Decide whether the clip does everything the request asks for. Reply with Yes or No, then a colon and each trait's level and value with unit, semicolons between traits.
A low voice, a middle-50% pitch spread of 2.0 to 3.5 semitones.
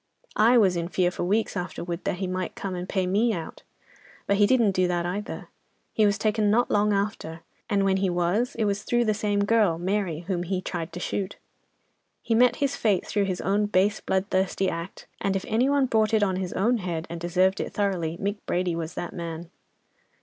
No: high, 195 Hz; average, 2.9 semitones